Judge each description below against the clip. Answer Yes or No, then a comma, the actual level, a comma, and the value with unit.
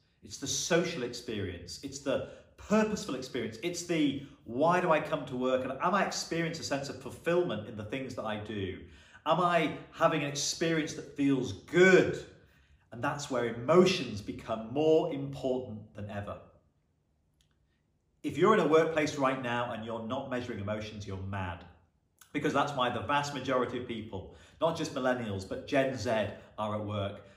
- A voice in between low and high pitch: No, low, 125 Hz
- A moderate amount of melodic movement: No, wide, 6.7 semitones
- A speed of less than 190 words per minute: Yes, average, 170 wpm